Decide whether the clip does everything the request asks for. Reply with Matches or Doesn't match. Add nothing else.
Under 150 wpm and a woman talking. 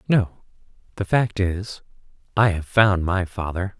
Doesn't match